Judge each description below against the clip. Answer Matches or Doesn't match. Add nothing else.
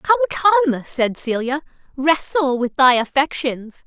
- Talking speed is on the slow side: Matches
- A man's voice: Doesn't match